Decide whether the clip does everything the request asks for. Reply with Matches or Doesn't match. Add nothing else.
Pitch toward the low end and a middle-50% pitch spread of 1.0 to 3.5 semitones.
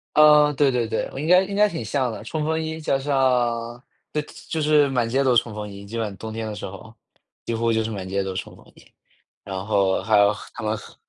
Doesn't match